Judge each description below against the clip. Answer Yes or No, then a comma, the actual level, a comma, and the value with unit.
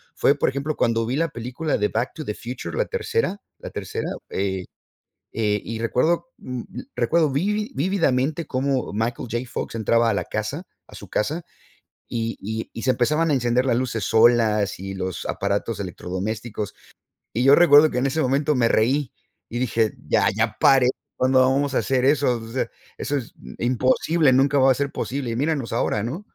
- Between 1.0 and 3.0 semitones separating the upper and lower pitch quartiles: No, average, 4.0 semitones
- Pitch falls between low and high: No, low, 125 Hz